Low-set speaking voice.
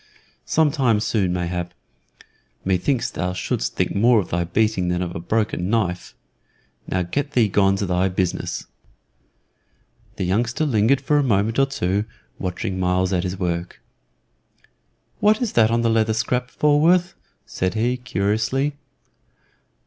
Yes: low, 105 Hz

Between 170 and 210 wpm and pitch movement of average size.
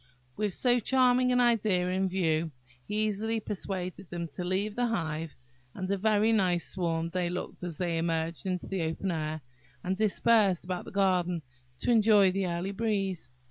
Yes: average, 175 wpm; average, 3.6 semitones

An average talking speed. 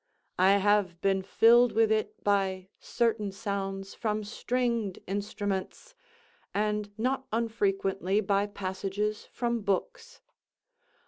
No: slow, 105 wpm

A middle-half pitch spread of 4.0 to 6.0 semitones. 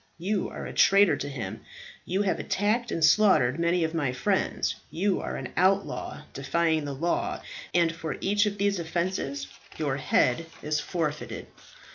Yes: average, 4.8 semitones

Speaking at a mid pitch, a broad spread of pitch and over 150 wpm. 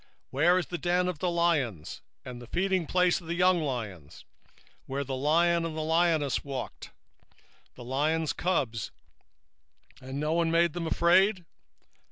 No: medium, 165 Hz; average, 4.3 semitones; average, 160 wpm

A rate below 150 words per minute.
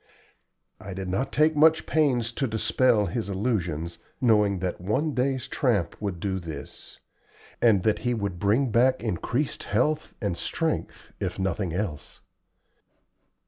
Yes: average, 140 wpm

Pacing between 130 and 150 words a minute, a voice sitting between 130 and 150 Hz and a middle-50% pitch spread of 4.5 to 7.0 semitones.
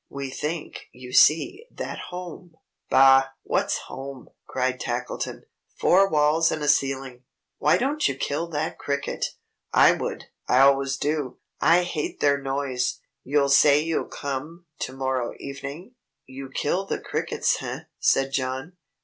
No: average, 145 wpm; medium, 140 Hz; average, 3.2 semitones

